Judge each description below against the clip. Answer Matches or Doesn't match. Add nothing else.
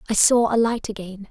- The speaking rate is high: Matches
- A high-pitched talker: Matches